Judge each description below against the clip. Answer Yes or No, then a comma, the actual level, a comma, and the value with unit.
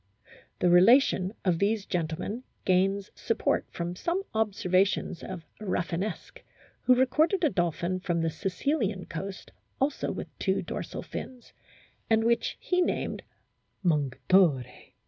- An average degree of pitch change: Yes, average, 4.8 semitones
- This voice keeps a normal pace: No, slow, 125 wpm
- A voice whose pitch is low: No, high, 190 Hz